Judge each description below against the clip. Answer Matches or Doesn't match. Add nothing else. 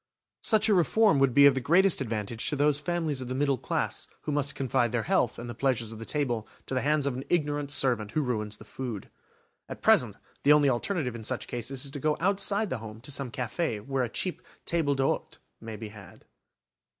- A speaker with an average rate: Doesn't match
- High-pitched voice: Doesn't match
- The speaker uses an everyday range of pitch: Matches